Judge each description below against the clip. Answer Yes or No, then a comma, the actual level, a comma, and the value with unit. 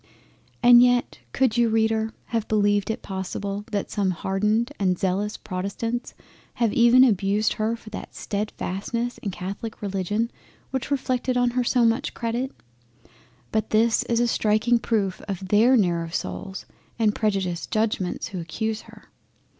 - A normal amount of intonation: Yes, average, 3.1 semitones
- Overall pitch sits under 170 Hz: No, high, 215 Hz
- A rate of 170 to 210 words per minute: No, average, 150 wpm